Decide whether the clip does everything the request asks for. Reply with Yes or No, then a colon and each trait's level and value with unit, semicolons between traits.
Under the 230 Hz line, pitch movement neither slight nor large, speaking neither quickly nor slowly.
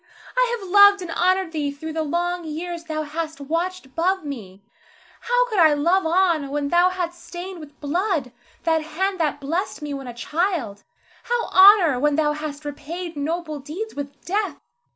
No: very high, 330 Hz; average, 3.9 semitones; average, 175 wpm